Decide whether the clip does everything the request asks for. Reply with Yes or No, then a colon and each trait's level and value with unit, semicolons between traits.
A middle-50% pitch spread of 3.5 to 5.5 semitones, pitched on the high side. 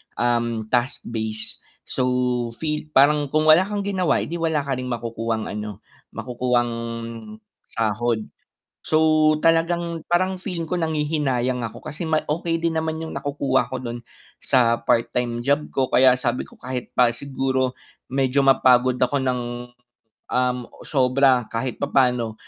No: average, 4.0 semitones; low, 130 Hz